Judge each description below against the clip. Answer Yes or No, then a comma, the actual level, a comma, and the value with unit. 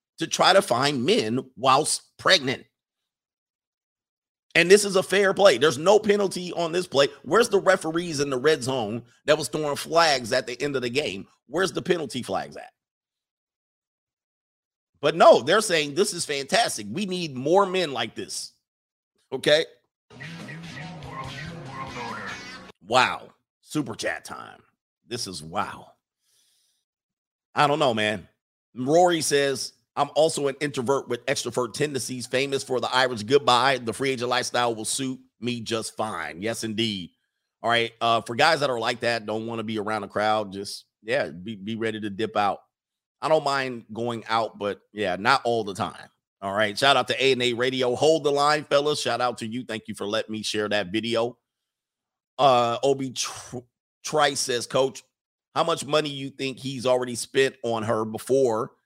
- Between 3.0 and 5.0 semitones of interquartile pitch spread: Yes, average, 4.2 semitones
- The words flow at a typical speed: Yes, average, 170 wpm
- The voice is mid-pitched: No, low, 130 Hz